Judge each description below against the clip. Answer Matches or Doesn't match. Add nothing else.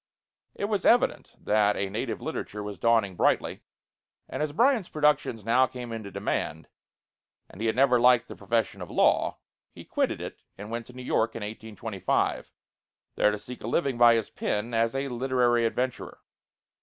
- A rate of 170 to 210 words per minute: Matches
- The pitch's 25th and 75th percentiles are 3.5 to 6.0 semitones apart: Doesn't match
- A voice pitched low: Matches